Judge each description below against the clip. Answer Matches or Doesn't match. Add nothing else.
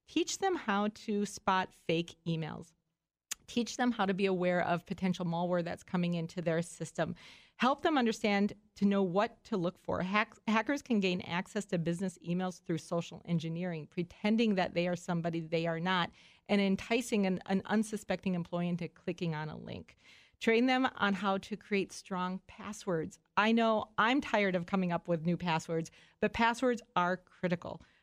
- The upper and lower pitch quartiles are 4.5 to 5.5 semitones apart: Doesn't match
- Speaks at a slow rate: Doesn't match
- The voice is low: Doesn't match